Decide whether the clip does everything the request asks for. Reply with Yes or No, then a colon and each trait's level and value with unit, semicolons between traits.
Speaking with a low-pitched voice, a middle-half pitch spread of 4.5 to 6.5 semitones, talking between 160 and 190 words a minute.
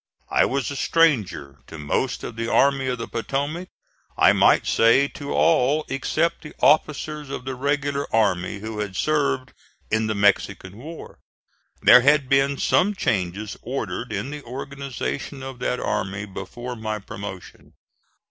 No: low, 130 Hz; average, 5.0 semitones; average, 150 wpm